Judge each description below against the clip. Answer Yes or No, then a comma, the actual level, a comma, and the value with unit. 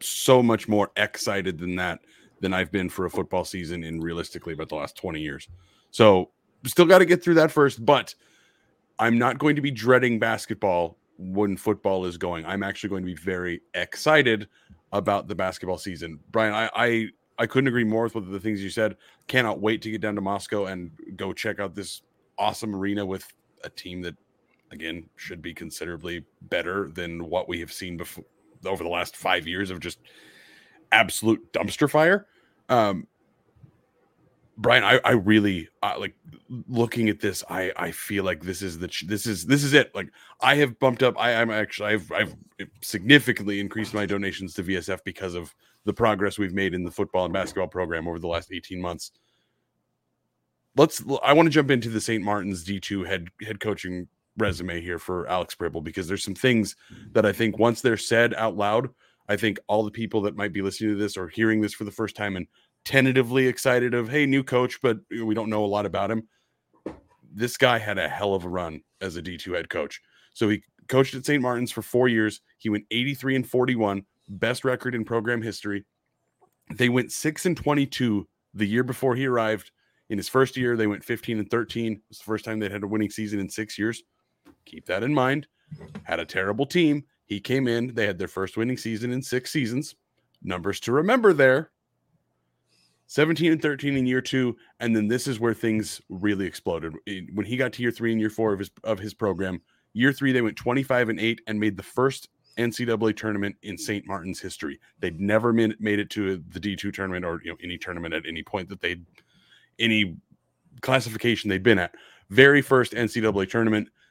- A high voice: No, low, 110 Hz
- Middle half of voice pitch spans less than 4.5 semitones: Yes, average, 4.0 semitones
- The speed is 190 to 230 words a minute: Yes, average, 200 wpm